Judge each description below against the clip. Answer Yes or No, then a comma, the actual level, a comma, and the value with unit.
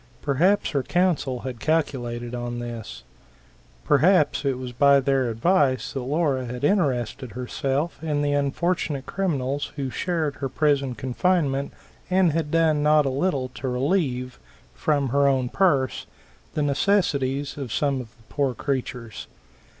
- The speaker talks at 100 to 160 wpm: Yes, average, 140 wpm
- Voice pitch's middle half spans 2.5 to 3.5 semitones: Yes, average, 3.2 semitones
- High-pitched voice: No, medium, 140 Hz